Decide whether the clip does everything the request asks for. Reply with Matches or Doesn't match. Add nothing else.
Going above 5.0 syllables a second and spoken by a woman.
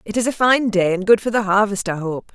Matches